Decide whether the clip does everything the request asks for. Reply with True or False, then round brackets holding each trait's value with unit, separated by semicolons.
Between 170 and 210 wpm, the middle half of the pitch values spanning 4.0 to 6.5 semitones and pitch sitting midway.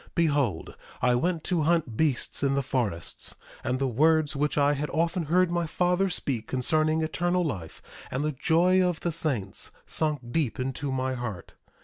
True (175 wpm; 4.3 semitones; 150 Hz)